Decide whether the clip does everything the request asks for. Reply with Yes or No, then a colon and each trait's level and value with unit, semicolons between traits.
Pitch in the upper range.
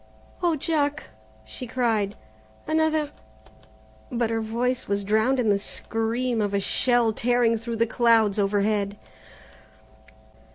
Yes: high, 225 Hz